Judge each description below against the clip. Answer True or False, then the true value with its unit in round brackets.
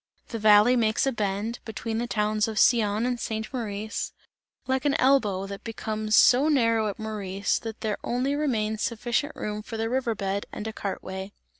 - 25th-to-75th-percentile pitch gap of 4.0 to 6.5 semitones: False (2.4 semitones)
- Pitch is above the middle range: True (220 Hz)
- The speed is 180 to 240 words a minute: True (185 wpm)